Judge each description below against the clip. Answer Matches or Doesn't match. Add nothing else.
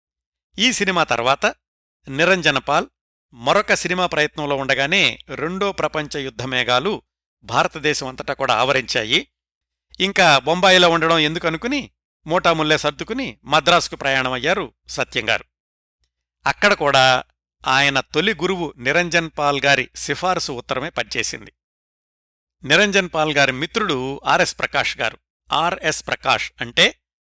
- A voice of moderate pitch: Matches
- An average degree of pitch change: Doesn't match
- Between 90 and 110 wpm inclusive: Matches